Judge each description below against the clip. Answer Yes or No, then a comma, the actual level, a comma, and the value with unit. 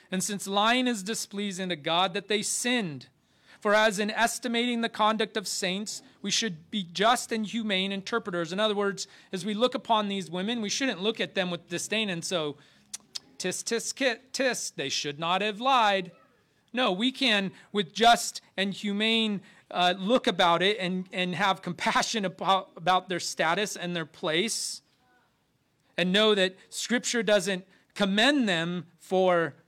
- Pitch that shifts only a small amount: No, average, 3.6 semitones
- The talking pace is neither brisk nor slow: Yes, average, 165 wpm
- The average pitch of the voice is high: Yes, high, 200 Hz